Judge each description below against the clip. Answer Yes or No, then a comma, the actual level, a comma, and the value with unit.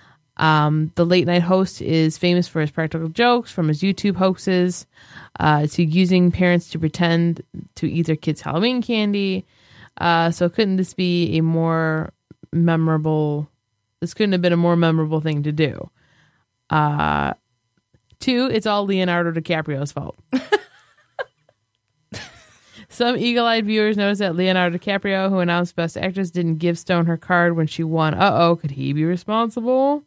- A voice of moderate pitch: Yes, medium, 170 Hz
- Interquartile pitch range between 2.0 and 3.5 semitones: Yes, average, 3.0 semitones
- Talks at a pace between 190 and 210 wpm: No, average, 155 wpm